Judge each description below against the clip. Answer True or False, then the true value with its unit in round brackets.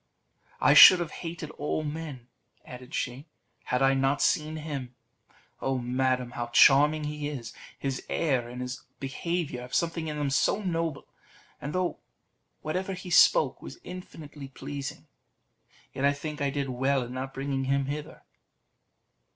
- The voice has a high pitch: False (140 Hz)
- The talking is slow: False (155 wpm)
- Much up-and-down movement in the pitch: False (3.0 semitones)